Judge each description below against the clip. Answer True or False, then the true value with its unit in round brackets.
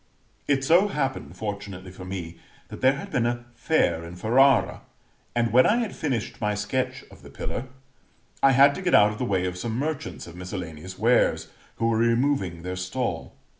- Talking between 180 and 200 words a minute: True (190 wpm)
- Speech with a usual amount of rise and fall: False (6.4 semitones)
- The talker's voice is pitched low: True (115 Hz)